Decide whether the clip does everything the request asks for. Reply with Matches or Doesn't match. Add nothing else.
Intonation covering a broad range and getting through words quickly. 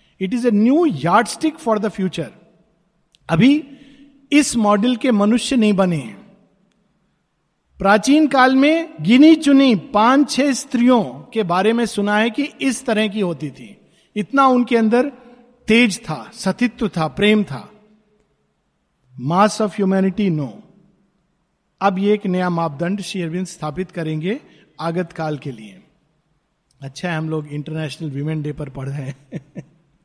Doesn't match